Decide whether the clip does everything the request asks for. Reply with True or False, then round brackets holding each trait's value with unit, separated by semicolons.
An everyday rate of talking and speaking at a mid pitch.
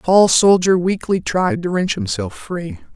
True (185 wpm; 155 Hz)